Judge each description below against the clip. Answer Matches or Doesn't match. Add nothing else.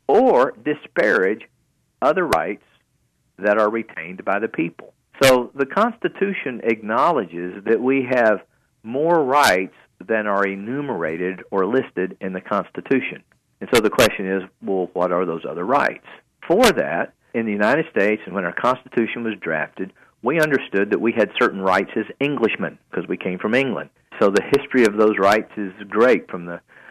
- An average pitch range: Matches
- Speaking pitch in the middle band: Doesn't match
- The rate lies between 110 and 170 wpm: Matches